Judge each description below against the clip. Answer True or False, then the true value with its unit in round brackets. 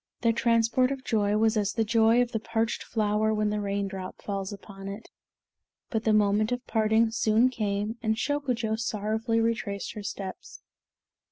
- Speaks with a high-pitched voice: True (220 Hz)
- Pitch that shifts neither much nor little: False (1.8 semitones)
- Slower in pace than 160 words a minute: False (165 wpm)